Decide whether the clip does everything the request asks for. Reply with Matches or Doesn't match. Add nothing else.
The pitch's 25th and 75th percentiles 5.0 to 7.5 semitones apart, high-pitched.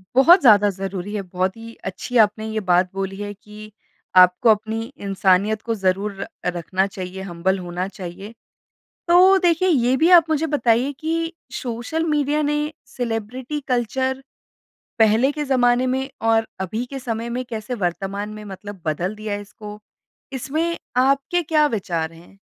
Matches